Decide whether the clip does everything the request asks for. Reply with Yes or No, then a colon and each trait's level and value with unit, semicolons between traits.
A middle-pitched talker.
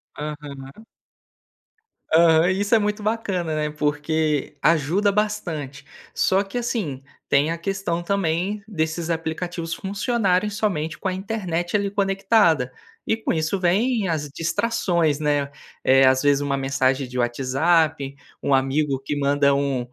Yes: medium, 165 Hz